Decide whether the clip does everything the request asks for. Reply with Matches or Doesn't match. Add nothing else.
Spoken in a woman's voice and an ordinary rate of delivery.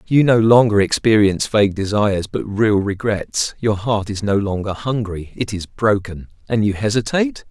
Doesn't match